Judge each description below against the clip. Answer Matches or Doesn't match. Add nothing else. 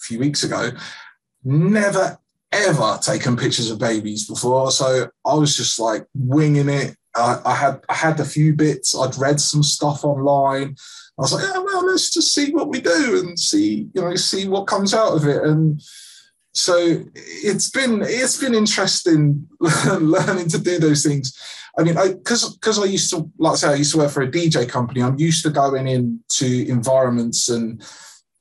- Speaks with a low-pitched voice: Doesn't match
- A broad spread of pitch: Matches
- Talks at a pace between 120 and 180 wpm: Doesn't match